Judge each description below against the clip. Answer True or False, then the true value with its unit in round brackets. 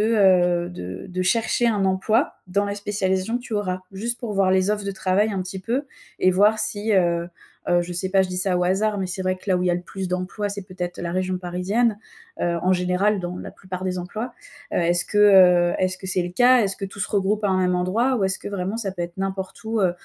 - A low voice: False (190 Hz)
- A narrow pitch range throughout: True (2.3 semitones)